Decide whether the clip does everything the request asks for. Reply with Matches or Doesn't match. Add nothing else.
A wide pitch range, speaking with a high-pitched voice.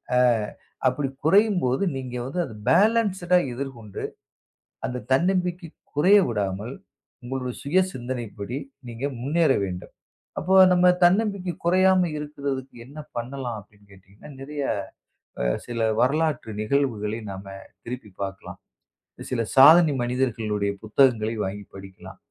Doesn't match